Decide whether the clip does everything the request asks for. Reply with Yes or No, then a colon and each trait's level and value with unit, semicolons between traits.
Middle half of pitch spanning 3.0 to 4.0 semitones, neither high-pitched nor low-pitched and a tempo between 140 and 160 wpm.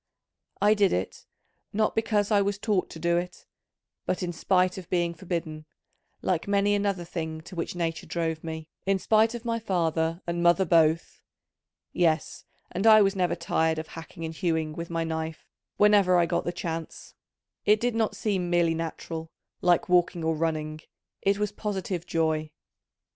No: average, 3.5 semitones; medium, 175 Hz; average, 170 wpm